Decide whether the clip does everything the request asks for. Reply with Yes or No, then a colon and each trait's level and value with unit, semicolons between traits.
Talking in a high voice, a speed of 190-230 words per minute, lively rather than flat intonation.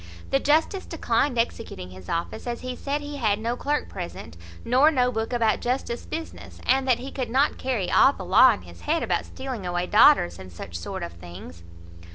Yes: high, 240 Hz; average, 200 wpm; wide, 7.4 semitones